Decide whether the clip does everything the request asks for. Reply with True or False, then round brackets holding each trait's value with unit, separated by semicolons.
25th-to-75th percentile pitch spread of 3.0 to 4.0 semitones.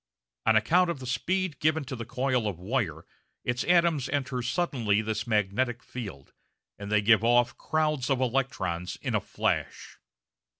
False (4.7 semitones)